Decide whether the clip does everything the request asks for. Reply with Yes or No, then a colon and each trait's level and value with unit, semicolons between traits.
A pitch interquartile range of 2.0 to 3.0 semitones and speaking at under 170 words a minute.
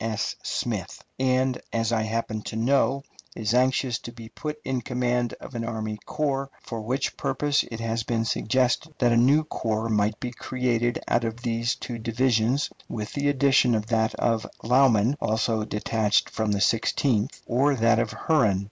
No: average, 2.7 semitones; average, 175 wpm